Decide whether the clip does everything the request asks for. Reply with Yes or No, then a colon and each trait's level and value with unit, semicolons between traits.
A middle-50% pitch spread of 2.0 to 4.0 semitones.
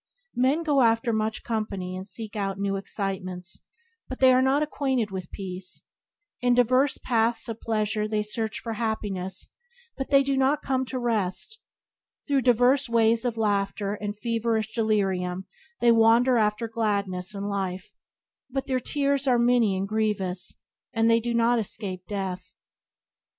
Yes: average, 3.7 semitones